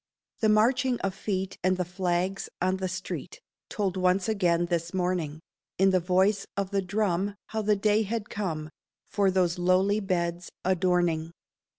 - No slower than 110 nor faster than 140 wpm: No, average, 160 wpm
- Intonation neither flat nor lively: No, narrow, 2.3 semitones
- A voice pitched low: No, medium, 185 Hz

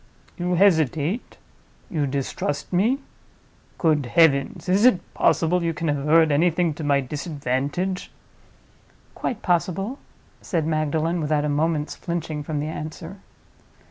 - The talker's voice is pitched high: No, medium, 160 Hz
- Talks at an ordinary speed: No, slow, 125 wpm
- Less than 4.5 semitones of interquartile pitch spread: Yes, average, 3.2 semitones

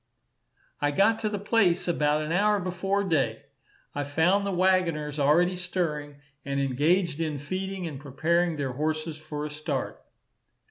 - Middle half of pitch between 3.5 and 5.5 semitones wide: Yes, average, 4.0 semitones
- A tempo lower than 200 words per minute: Yes, average, 150 wpm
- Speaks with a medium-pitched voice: Yes, medium, 160 Hz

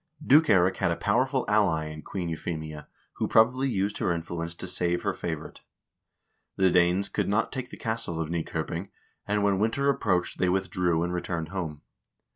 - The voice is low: Yes, very low, 90 Hz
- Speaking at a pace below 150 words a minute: No, average, 175 wpm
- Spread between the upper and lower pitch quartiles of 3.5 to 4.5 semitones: Yes, average, 3.8 semitones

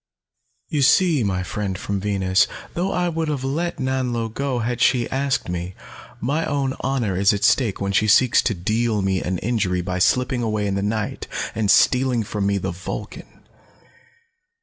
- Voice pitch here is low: Yes, low, 110 Hz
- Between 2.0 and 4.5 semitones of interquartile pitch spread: No, average, 5.2 semitones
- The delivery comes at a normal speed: Yes, average, 175 wpm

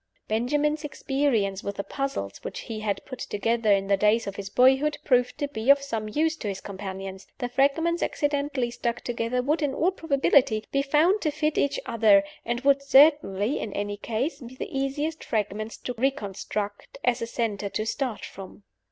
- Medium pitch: No, high, 245 Hz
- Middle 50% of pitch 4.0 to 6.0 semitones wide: Yes, average, 5.2 semitones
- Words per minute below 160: No, average, 185 wpm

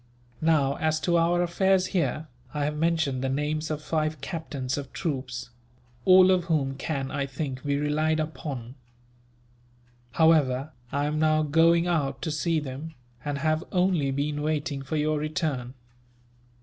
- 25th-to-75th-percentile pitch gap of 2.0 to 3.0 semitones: Yes, narrow, 2.6 semitones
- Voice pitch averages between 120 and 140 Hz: No, medium, 155 Hz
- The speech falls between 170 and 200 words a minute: No, average, 150 wpm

